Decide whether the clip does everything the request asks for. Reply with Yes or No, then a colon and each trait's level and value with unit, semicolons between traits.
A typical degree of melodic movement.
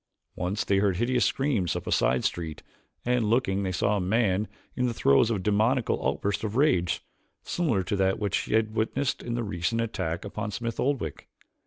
Yes: average, 4.1 semitones